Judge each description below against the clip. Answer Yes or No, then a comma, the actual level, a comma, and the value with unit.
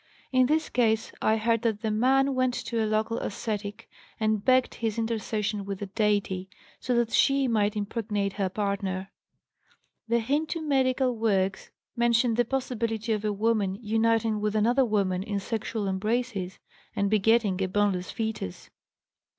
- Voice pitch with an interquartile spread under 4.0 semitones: Yes, narrow, 2.6 semitones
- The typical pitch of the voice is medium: No, high, 220 Hz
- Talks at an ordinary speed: Yes, average, 150 wpm